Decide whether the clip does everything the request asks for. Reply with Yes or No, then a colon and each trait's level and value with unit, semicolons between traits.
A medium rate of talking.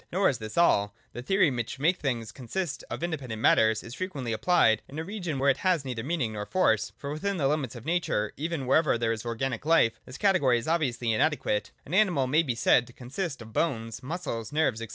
No: fast, 220 wpm